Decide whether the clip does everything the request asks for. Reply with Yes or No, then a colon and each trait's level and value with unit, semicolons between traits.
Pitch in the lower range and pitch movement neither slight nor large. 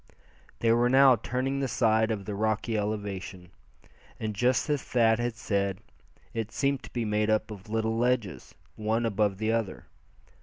No: low, 110 Hz; narrow, 2.3 semitones